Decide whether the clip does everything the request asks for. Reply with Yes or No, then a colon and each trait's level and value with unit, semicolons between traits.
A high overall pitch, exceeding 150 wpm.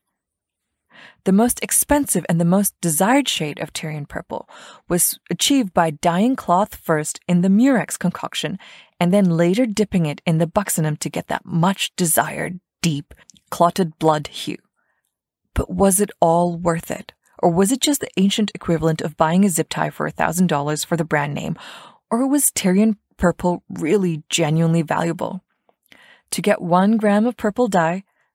No: medium, 175 Hz; average, 165 wpm